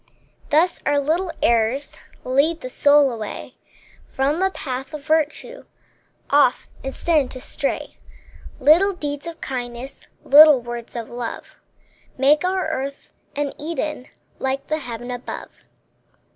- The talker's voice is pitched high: Yes, very high, 280 Hz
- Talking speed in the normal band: No, slow, 130 wpm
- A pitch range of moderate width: Yes, average, 3.5 semitones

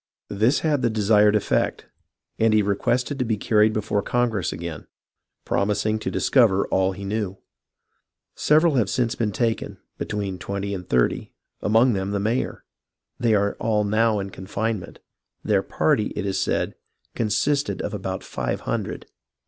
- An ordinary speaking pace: Yes, average, 160 wpm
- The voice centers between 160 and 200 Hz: No, low, 105 Hz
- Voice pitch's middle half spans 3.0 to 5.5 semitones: No, narrow, 2.5 semitones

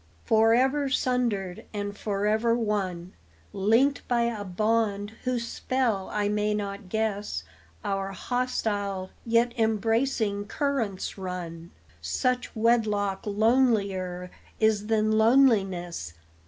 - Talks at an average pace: No, slow, 100 wpm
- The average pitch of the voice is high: Yes, high, 210 Hz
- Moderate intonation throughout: Yes, average, 3.0 semitones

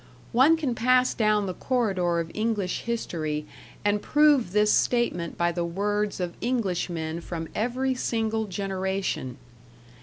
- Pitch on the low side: No, high, 205 Hz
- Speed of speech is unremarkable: No, slow, 130 wpm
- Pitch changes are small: No, average, 5.3 semitones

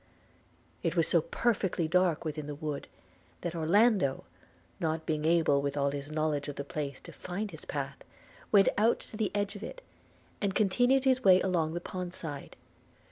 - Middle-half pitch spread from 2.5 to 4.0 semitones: No, wide, 5.4 semitones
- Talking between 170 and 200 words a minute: Yes, average, 180 wpm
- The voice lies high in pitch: No, medium, 170 Hz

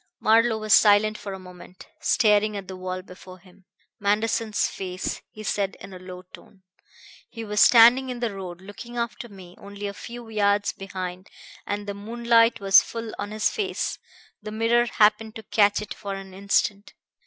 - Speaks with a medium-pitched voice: No, high, 205 Hz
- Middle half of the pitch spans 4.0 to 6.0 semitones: No, average, 2.7 semitones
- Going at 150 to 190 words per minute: Yes, average, 175 wpm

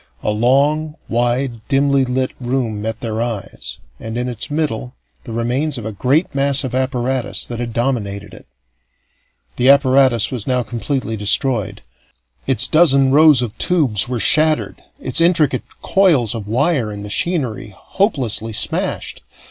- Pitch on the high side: No, low, 125 Hz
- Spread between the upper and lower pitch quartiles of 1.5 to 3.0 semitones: No, average, 3.6 semitones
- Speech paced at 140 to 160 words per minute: Yes, average, 145 wpm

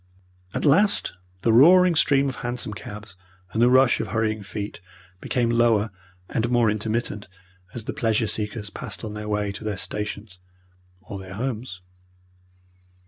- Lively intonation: No, average, 2.7 semitones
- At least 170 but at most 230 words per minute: No, average, 150 wpm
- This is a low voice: Yes, low, 110 Hz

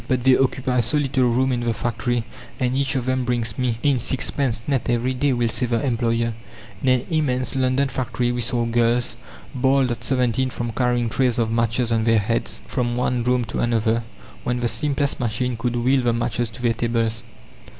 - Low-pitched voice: Yes, low, 120 Hz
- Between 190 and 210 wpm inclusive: Yes, average, 200 wpm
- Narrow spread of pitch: Yes, narrow, 1.8 semitones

